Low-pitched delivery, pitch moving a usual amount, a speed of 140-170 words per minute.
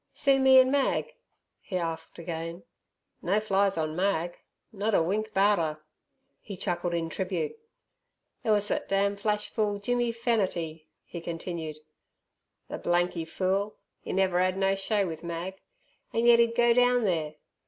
No: high, 195 Hz; average, 4.1 semitones; average, 160 wpm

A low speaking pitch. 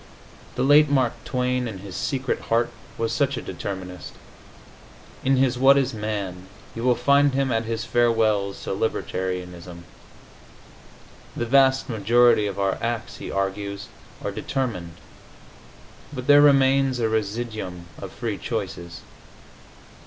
Yes: low, 115 Hz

